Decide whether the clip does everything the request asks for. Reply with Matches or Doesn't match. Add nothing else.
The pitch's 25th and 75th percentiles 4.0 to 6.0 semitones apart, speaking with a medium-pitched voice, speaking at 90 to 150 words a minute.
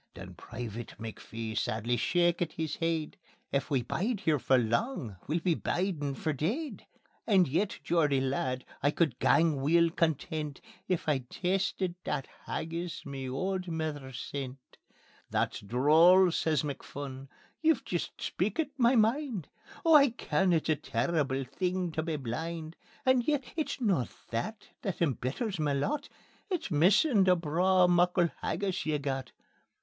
Matches